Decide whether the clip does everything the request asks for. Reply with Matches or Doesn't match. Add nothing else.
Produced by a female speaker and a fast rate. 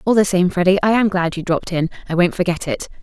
Matches